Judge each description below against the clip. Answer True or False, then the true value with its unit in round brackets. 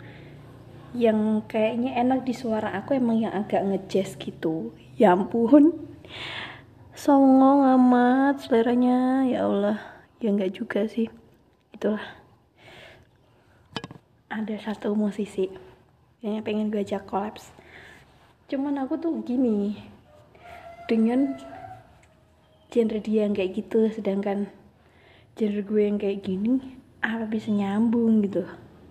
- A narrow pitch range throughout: False (3.7 semitones)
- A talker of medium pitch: False (220 Hz)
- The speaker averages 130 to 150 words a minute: False (105 wpm)